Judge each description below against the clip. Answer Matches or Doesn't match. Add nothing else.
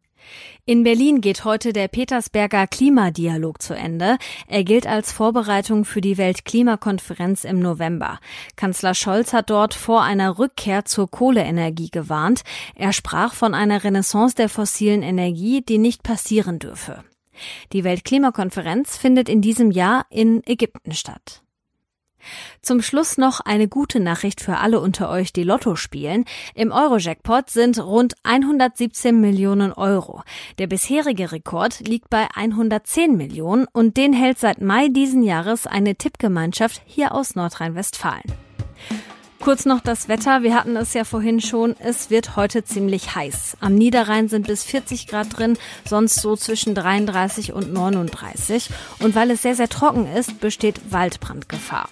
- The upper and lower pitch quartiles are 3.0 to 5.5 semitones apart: Matches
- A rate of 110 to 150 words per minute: Matches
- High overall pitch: Matches